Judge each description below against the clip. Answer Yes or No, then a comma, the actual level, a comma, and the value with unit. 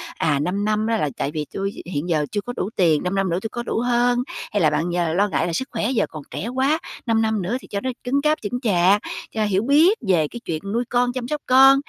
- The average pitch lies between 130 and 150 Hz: No, high, 215 Hz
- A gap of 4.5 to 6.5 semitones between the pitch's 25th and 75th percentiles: Yes, wide, 5.6 semitones